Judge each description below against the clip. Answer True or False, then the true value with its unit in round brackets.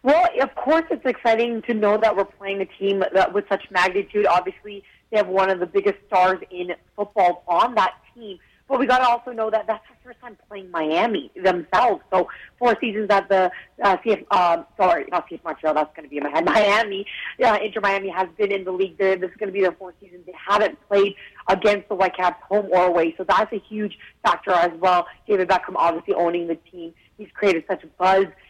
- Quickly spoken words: True (225 wpm)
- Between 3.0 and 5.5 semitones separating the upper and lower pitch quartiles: False (2.5 semitones)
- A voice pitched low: False (195 Hz)